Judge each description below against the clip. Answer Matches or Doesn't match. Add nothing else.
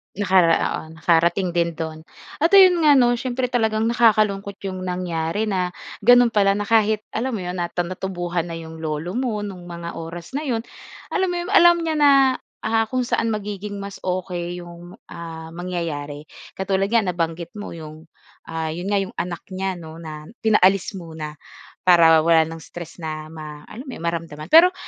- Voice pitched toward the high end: Doesn't match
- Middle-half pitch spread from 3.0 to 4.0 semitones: Doesn't match